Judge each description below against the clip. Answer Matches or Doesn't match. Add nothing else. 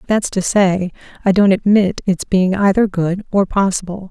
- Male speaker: Doesn't match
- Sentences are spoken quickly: Doesn't match